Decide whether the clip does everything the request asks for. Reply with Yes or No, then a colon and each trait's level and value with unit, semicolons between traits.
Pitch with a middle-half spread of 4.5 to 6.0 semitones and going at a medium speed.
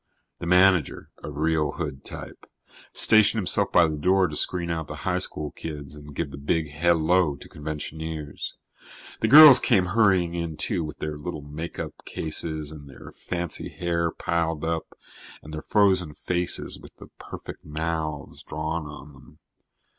No: narrow, 2.6 semitones; average, 160 wpm